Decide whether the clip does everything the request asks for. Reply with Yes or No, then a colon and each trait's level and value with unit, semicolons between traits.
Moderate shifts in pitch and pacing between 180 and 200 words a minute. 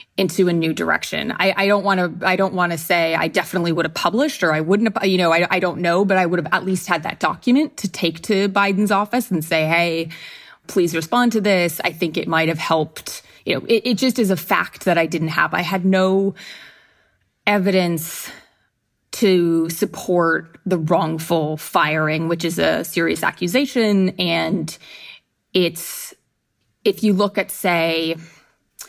Yes: average, 3.2 semitones; average, 185 wpm